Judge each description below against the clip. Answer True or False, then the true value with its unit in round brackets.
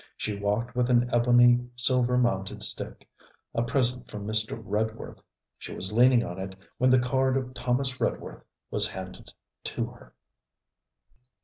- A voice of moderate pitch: False (120 Hz)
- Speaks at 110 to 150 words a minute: True (145 wpm)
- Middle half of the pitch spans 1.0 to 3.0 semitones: True (2.7 semitones)